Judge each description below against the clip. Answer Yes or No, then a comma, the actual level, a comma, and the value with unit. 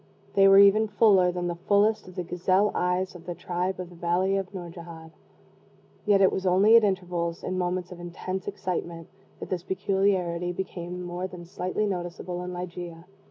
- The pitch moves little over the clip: Yes, narrow, 1.6 semitones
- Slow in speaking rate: No, average, 180 wpm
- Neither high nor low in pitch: Yes, medium, 180 Hz